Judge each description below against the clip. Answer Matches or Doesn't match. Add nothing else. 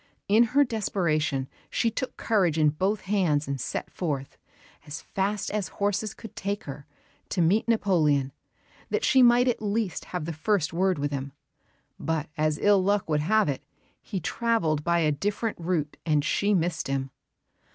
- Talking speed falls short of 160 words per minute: Doesn't match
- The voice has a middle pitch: Matches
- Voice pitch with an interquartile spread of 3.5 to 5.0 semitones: Doesn't match